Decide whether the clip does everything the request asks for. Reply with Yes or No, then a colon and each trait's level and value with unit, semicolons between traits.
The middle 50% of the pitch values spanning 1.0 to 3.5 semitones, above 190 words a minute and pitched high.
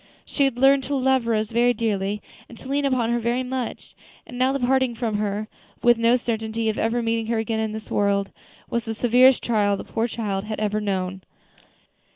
Yes: narrow, 2.5 semitones; fast, 205 wpm; high, 230 Hz